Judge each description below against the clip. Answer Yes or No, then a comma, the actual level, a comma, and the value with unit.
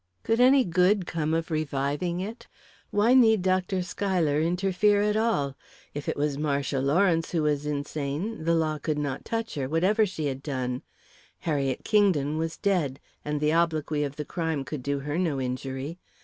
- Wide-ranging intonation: No, average, 4.6 semitones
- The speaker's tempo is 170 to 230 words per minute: Yes, average, 175 wpm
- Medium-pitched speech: Yes, medium, 160 Hz